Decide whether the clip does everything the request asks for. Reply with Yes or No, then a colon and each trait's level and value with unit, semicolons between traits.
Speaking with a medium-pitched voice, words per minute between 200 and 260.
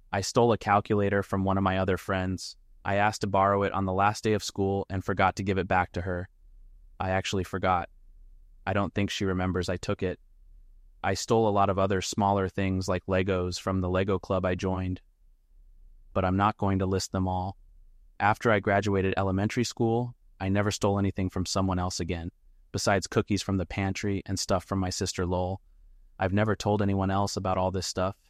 No: very low, 95 Hz; fast, 205 wpm